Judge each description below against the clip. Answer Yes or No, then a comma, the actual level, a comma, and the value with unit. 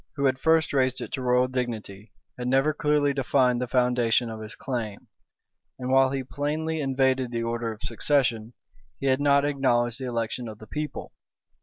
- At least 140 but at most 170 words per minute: No, average, 180 wpm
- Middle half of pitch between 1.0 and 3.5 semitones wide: Yes, average, 2.7 semitones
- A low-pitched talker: Yes, low, 130 Hz